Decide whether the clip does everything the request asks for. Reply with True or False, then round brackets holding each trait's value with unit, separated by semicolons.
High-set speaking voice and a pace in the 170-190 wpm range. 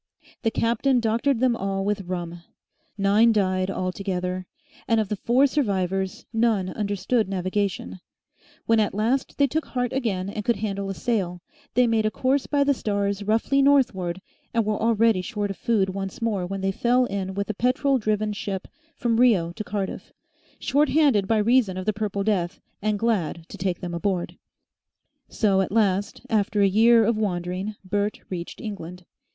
True (205 Hz; 175 wpm)